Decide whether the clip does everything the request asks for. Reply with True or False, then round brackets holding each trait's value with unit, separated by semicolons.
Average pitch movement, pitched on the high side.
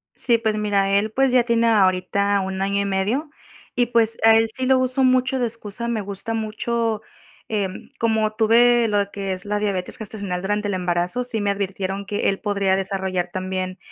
True (3.0 semitones; 210 Hz)